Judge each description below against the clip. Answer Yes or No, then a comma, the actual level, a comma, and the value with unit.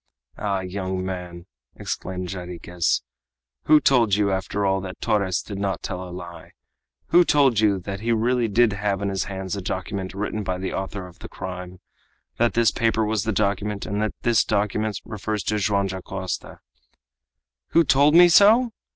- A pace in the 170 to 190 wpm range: Yes, average, 175 wpm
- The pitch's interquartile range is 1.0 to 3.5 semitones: Yes, average, 2.8 semitones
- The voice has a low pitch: Yes, low, 100 Hz